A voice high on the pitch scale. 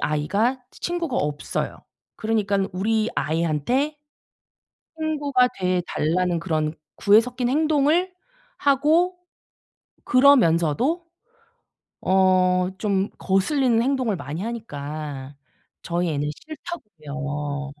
Yes: high, 205 Hz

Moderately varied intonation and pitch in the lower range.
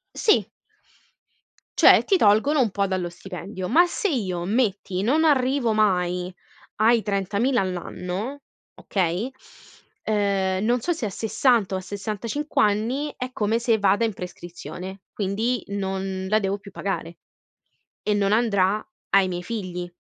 No: average, 3.7 semitones; high, 205 Hz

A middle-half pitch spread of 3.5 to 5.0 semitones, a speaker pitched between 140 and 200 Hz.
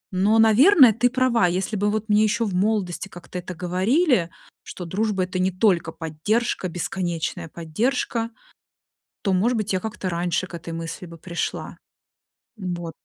Yes: average, 4.0 semitones; high, 190 Hz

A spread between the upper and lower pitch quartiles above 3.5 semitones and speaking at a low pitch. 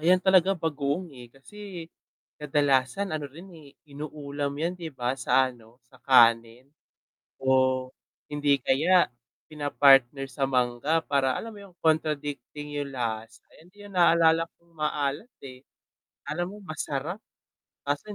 No: average, 4.0 semitones; medium, 145 Hz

